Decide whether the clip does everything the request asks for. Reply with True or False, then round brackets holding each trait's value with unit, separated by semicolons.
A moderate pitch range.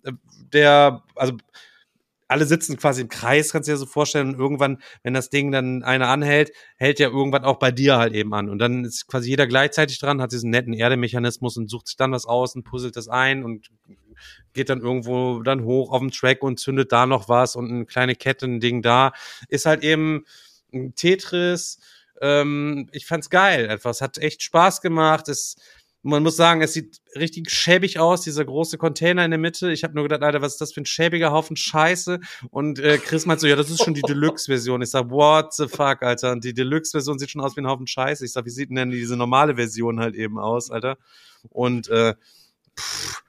True (3.6 semitones)